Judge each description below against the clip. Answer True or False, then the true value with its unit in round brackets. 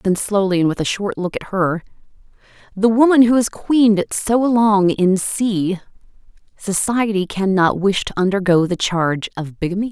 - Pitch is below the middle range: False (195 Hz)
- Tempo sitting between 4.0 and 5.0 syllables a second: True (4.8 syllables/s)